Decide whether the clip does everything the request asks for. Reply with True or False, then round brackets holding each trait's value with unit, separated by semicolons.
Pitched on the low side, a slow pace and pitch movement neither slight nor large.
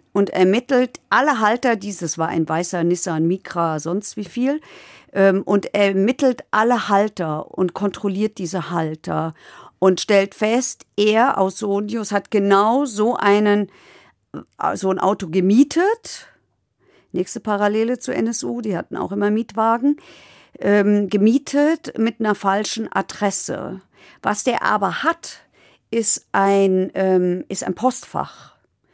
False (205 Hz; 120 wpm; 3.3 semitones)